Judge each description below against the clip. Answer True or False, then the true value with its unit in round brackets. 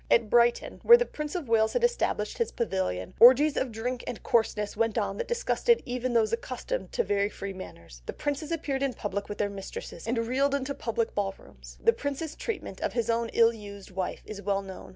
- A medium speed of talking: False (215 wpm)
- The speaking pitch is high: True (230 Hz)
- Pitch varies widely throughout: True (5.7 semitones)